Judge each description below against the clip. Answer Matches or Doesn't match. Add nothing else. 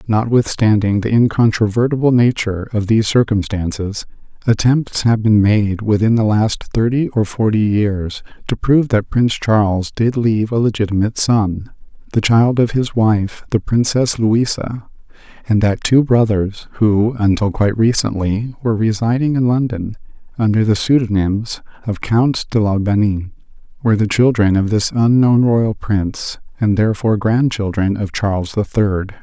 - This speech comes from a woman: Doesn't match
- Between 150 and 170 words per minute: Doesn't match